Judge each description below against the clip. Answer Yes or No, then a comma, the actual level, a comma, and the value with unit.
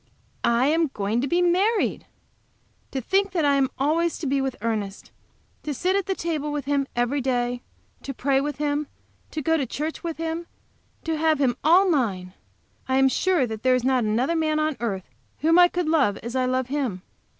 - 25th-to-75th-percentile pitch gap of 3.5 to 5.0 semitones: Yes, average, 4.4 semitones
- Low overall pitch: No, very high, 280 Hz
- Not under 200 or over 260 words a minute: Yes, fast, 205 wpm